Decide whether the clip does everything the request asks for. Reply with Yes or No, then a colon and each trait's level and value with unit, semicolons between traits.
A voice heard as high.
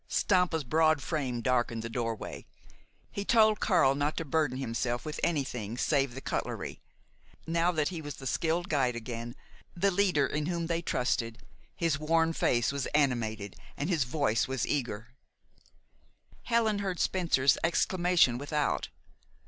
No: medium, 145 Hz